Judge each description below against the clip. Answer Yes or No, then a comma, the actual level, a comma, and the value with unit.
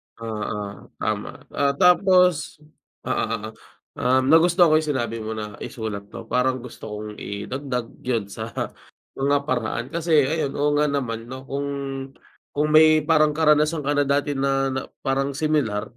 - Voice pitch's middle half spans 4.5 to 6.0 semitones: Yes, average, 4.9 semitones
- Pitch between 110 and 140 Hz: Yes, low, 135 Hz